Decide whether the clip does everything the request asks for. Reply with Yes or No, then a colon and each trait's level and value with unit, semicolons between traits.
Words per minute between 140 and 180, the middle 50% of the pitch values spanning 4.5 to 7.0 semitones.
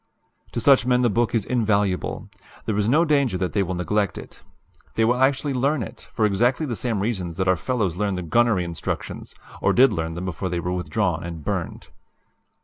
No: fast, 205 wpm; average, 5.2 semitones